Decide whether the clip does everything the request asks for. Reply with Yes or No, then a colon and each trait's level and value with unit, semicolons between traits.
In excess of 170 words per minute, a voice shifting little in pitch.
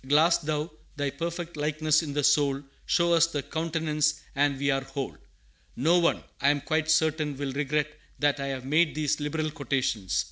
Yes: average, 180 wpm; narrow, 2.0 semitones